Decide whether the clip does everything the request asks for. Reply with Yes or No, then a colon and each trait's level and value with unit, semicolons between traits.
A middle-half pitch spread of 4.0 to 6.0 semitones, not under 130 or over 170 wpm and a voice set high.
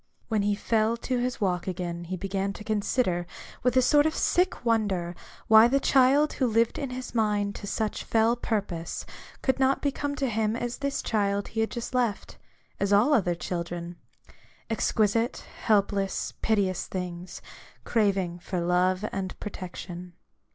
Yes: average, 4.4 semitones; average, 160 wpm; high, 210 Hz